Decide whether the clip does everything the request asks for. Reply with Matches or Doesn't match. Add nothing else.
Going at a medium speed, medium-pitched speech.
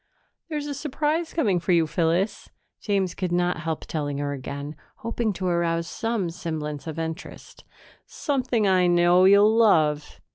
Matches